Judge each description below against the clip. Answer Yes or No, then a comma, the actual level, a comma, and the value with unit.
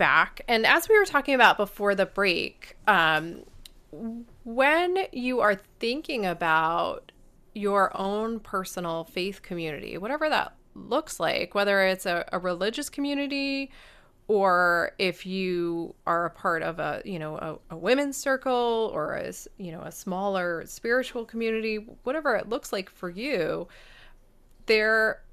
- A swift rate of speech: No, average, 140 wpm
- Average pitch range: No, wide, 5.7 semitones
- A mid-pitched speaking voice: No, high, 205 Hz